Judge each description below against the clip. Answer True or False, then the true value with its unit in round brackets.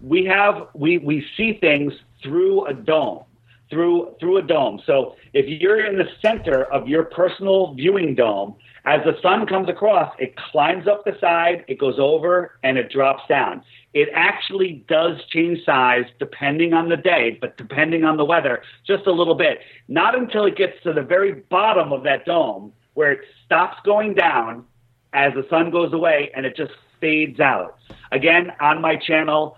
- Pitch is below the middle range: False (170 Hz)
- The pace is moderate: True (180 wpm)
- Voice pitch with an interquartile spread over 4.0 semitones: True (5.1 semitones)